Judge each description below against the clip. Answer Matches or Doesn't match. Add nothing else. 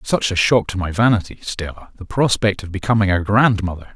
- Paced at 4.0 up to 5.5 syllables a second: Doesn't match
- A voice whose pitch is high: Doesn't match